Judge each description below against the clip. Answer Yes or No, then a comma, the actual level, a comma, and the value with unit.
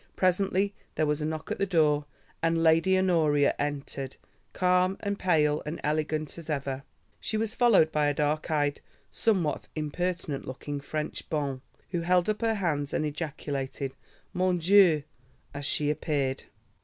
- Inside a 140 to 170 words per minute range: Yes, average, 155 wpm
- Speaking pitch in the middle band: Yes, medium, 155 Hz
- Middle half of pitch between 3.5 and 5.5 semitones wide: Yes, average, 3.8 semitones